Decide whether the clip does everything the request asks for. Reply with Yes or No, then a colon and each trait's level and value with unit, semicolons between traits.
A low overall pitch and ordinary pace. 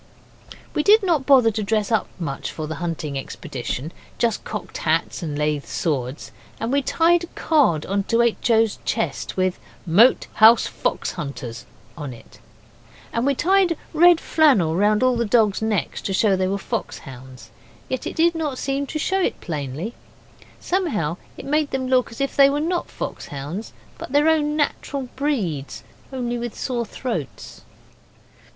No: high, 230 Hz; average, 170 wpm